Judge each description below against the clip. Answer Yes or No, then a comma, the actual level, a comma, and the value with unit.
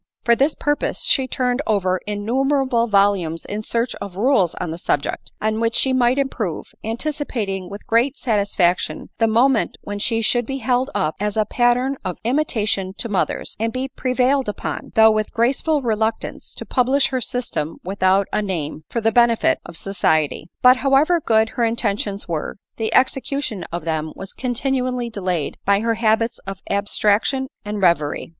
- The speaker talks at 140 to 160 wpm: No, average, 175 wpm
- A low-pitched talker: No, high, 225 Hz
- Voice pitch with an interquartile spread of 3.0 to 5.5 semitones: Yes, average, 4.3 semitones